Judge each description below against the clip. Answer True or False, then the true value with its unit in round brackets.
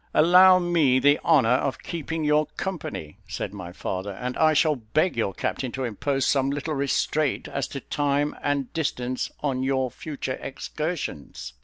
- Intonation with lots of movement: False (3.4 semitones)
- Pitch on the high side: False (140 Hz)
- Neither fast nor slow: True (160 wpm)